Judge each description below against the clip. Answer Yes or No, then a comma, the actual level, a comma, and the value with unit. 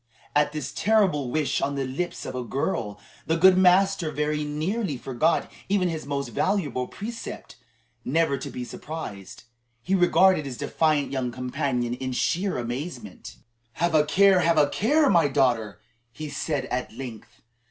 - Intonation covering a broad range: Yes, wide, 5.8 semitones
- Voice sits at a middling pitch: Yes, medium, 150 Hz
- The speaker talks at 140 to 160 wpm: Yes, average, 155 wpm